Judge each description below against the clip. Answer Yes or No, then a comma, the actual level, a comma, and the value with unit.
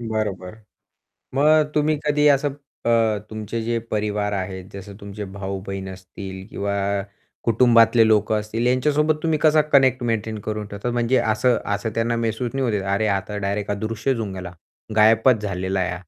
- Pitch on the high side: No, low, 110 Hz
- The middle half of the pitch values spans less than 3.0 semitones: No, average, 3.4 semitones